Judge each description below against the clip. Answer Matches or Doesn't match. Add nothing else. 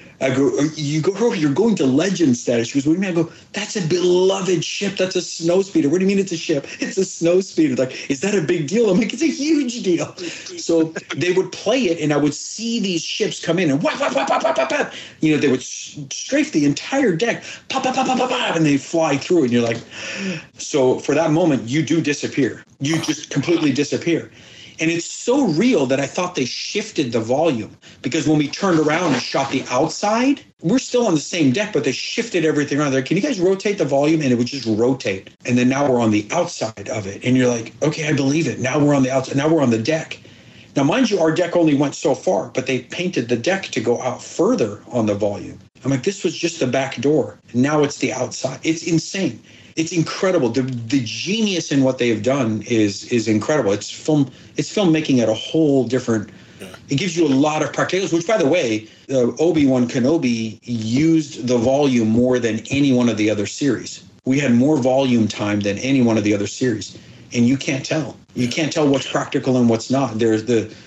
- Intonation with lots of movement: Matches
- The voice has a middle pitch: Matches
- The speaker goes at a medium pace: Doesn't match